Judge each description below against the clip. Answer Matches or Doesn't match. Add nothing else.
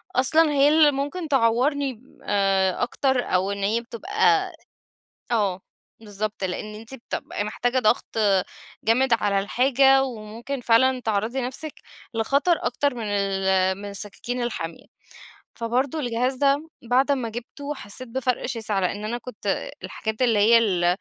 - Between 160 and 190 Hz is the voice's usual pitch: Doesn't match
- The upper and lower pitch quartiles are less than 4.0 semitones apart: Doesn't match